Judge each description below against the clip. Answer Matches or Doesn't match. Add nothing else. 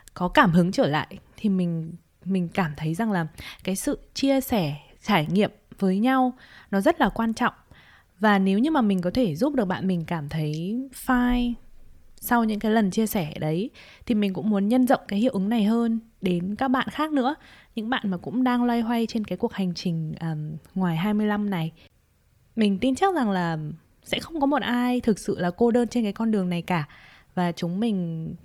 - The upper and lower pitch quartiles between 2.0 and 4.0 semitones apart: Doesn't match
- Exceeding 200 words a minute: Matches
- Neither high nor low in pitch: Doesn't match